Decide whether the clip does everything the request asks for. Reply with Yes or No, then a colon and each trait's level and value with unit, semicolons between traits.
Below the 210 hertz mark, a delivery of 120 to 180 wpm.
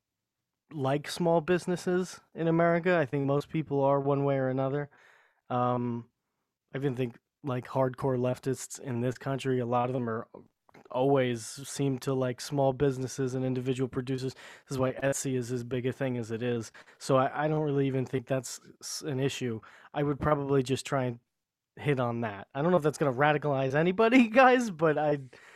No: low, 135 Hz; average, 190 wpm